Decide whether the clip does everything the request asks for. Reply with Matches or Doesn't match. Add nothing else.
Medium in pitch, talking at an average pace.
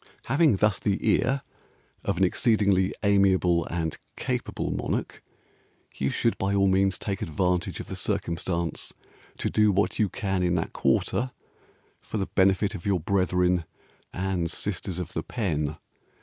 Doesn't match